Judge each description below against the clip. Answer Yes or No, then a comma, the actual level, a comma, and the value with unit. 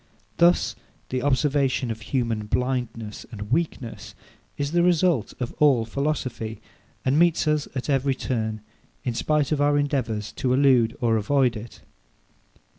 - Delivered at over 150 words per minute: No, average, 140 wpm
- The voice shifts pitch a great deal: No, average, 4.0 semitones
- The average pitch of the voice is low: Yes, low, 130 Hz